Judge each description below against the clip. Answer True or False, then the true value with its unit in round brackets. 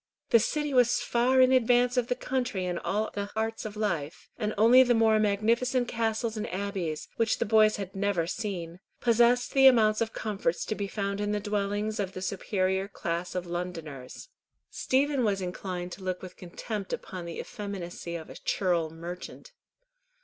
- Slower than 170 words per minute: False (180 wpm)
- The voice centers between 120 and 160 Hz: False (205 Hz)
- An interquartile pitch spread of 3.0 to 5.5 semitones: True (4.1 semitones)